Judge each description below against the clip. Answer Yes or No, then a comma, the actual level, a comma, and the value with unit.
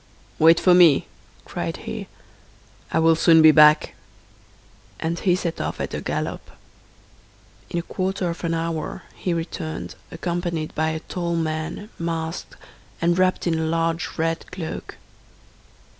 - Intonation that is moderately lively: No, narrow, 1.3 semitones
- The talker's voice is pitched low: No, medium, 165 Hz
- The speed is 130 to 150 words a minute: Yes, average, 145 wpm